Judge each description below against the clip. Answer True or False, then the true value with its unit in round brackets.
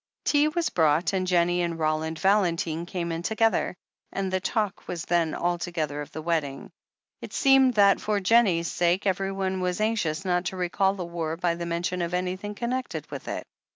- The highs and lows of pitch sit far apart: False (2.7 semitones)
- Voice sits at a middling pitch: True (180 Hz)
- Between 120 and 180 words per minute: False (190 wpm)